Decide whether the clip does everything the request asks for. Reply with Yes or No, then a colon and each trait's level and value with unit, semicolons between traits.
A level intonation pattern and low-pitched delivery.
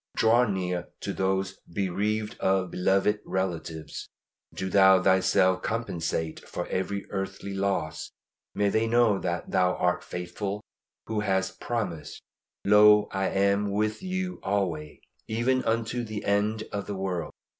Yes: narrow, 2.3 semitones; low, 100 Hz